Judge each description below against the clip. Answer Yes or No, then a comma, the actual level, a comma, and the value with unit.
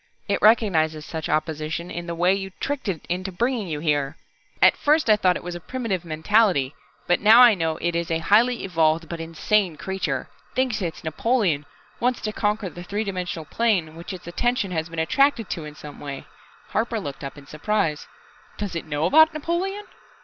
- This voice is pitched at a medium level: Yes, medium, 180 Hz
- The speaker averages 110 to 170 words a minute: No, average, 195 wpm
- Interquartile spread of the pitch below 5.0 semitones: No, average, 5.3 semitones